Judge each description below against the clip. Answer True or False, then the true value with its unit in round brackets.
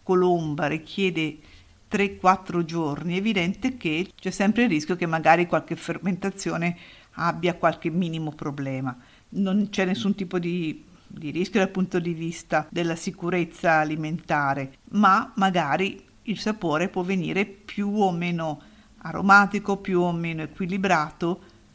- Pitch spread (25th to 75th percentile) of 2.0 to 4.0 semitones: True (3.1 semitones)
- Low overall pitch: False (175 Hz)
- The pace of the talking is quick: False (130 wpm)